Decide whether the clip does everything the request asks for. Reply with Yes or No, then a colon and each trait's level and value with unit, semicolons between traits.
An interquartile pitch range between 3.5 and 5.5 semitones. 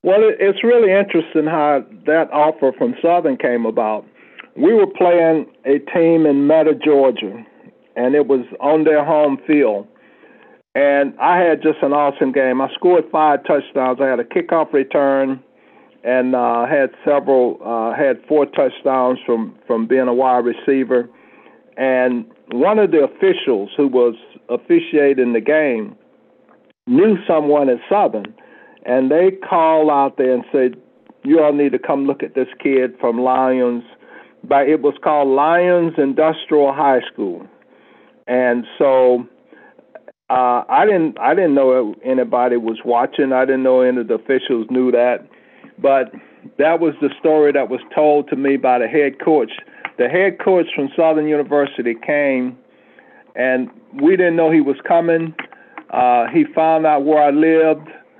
Yes: average, 4.0 semitones